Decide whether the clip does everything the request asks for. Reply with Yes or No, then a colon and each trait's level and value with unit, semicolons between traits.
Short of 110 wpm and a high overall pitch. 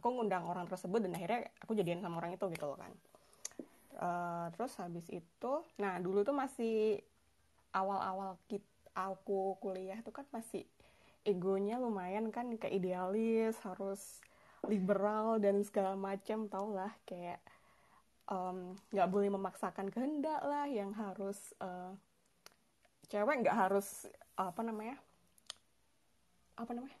No: average, 130 wpm; high, 195 Hz